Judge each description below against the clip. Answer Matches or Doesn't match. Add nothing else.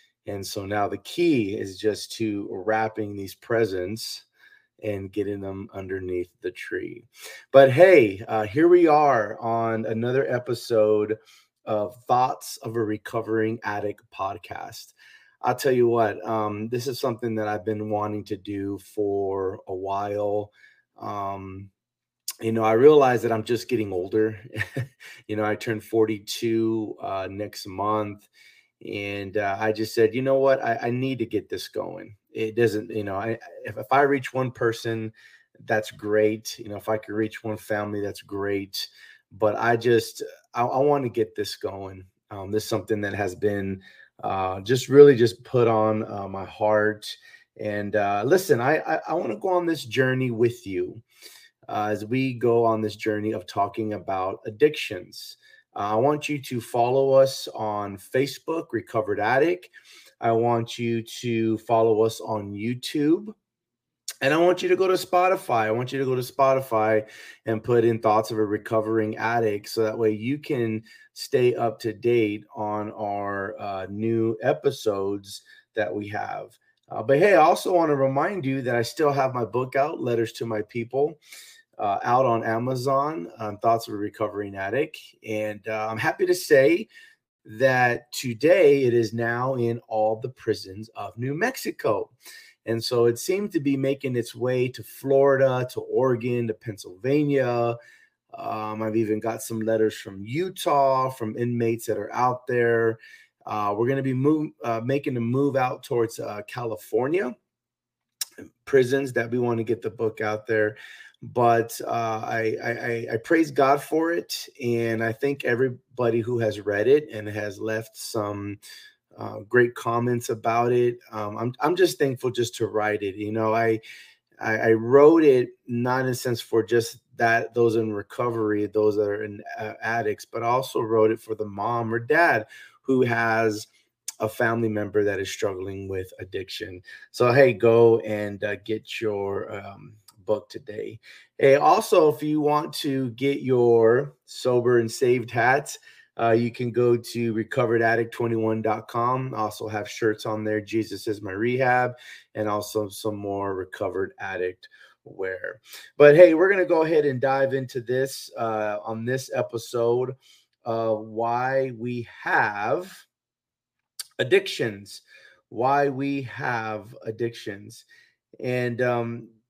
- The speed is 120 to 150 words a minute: Doesn't match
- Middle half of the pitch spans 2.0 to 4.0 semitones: Matches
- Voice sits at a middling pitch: Doesn't match